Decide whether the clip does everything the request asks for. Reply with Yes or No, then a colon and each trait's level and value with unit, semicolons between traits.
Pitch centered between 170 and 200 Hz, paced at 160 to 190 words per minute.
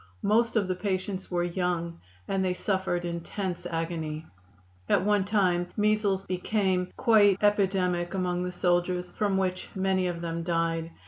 No: medium, 185 Hz; average, 145 wpm